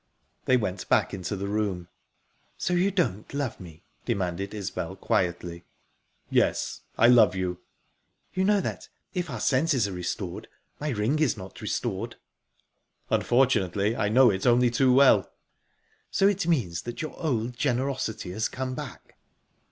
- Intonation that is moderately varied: No, wide, 6.1 semitones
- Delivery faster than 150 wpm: No, average, 145 wpm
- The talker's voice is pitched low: Yes, low, 115 Hz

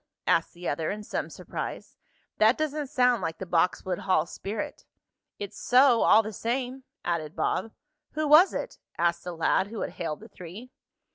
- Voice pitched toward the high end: Yes, high, 210 Hz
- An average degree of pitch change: No, wide, 6.4 semitones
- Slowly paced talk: No, average, 170 wpm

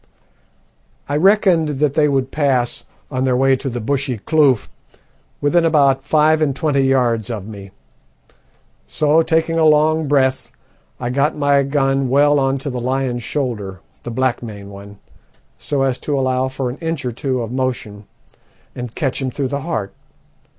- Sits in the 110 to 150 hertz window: Yes, low, 135 Hz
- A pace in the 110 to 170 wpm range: Yes, average, 165 wpm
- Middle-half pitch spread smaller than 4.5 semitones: Yes, average, 3.0 semitones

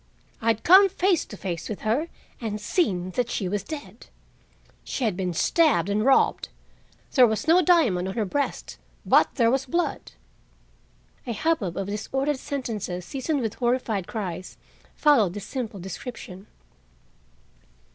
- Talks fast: No, average, 145 wpm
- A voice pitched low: No, high, 225 Hz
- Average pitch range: No, wide, 6.2 semitones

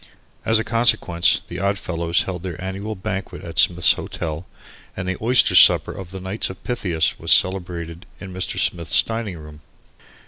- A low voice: Yes, very low, 95 Hz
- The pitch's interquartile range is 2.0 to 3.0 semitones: Yes, narrow, 2.6 semitones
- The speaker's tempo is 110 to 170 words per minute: Yes, average, 165 wpm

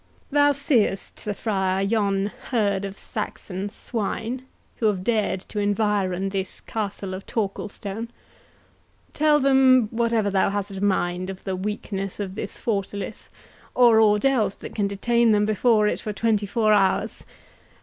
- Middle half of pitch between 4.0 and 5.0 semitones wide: No, narrow, 2.6 semitones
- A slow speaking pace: No, average, 145 wpm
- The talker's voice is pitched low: No, high, 205 Hz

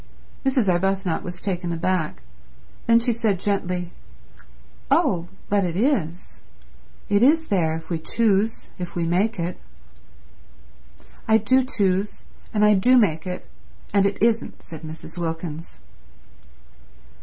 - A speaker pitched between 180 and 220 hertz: Yes, high, 190 Hz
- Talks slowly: Yes, slow, 130 wpm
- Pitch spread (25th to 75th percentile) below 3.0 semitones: No, average, 4.2 semitones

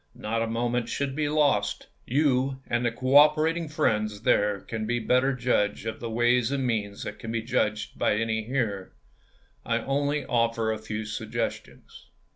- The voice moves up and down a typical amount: Yes, average, 3.5 semitones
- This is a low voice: Yes, low, 115 Hz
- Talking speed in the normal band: Yes, average, 160 wpm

